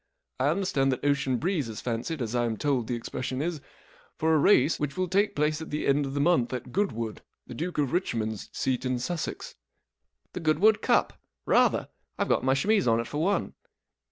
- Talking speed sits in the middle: No, fast, 215 wpm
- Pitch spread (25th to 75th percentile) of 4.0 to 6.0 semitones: Yes, average, 5.0 semitones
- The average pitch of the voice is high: No, medium, 140 Hz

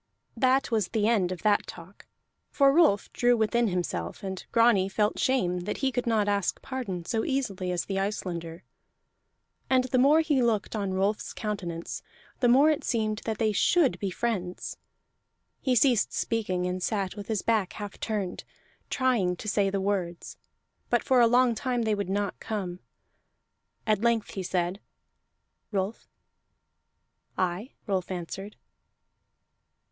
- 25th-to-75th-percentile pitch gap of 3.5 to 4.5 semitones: Yes, average, 4.1 semitones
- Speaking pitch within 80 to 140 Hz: No, high, 210 Hz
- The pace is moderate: Yes, average, 150 wpm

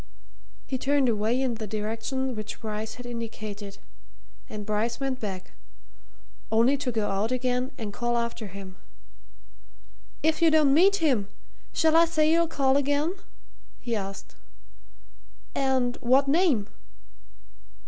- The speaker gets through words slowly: Yes, slow, 130 wpm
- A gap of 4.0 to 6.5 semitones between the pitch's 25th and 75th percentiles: Yes, average, 4.5 semitones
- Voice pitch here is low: No, high, 245 Hz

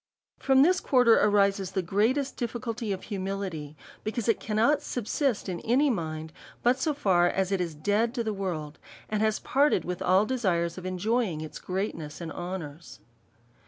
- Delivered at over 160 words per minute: Yes, average, 170 wpm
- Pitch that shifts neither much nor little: Yes, average, 4.9 semitones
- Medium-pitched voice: No, high, 200 Hz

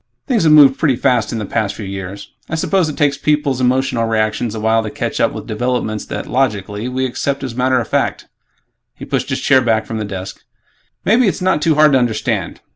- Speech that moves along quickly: Yes, fast, 220 wpm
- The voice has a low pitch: Yes, low, 125 Hz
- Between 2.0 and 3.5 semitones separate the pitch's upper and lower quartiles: No, average, 4.6 semitones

